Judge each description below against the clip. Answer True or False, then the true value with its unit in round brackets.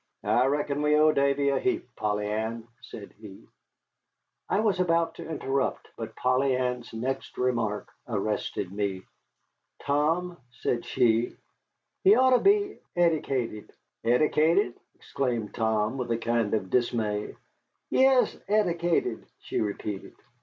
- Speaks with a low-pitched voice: True (125 Hz)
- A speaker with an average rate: False (125 wpm)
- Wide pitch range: True (6.5 semitones)